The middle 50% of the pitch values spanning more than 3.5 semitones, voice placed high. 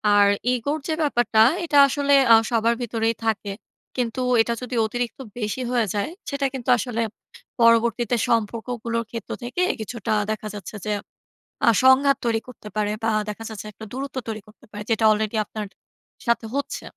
No: narrow, 2.4 semitones; high, 230 Hz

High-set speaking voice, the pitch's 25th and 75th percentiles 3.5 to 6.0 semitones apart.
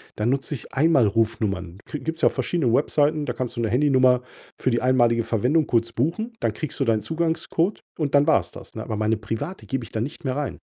No: low, 130 Hz; average, 4.7 semitones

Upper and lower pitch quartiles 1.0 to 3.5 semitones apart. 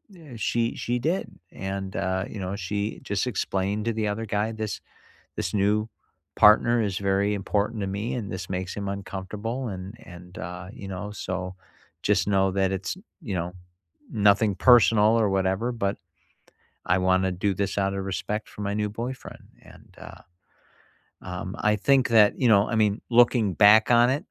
Yes: narrow, 2.5 semitones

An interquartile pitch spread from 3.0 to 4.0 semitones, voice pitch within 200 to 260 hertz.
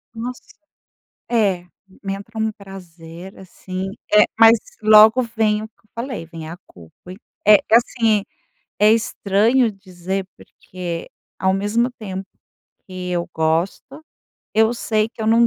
Yes: average, 3.5 semitones; high, 210 Hz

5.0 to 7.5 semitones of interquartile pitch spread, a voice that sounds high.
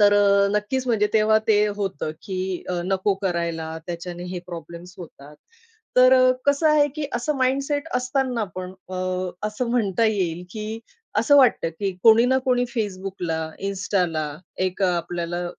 Yes: wide, 5.5 semitones; high, 205 Hz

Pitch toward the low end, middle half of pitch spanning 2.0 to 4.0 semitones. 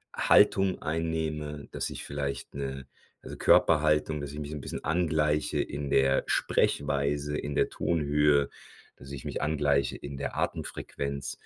No: very low, 75 Hz; narrow, 1.5 semitones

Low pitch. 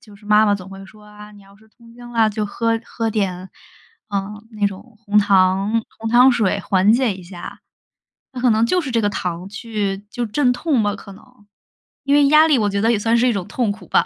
No: high, 215 Hz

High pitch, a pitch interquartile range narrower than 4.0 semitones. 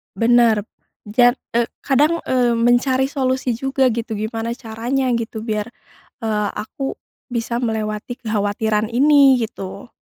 Yes: high, 235 Hz; average, 2.8 semitones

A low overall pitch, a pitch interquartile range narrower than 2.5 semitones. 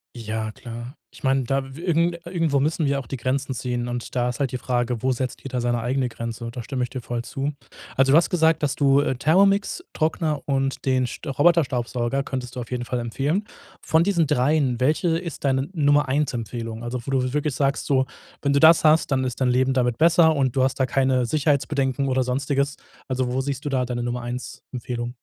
No: low, 130 Hz; average, 2.8 semitones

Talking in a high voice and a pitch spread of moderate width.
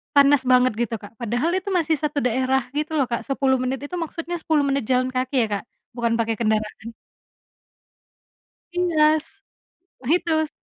Yes: very high, 275 Hz; average, 4.1 semitones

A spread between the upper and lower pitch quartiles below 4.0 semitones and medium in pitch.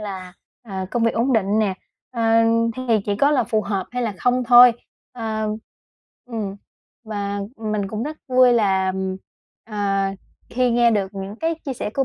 No: average, 3.5 semitones; high, 220 Hz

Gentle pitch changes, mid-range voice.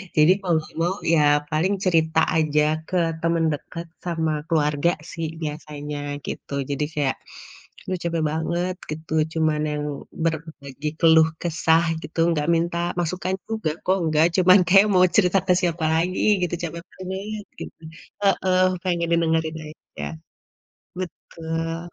Yes: narrow, 2.2 semitones; medium, 165 Hz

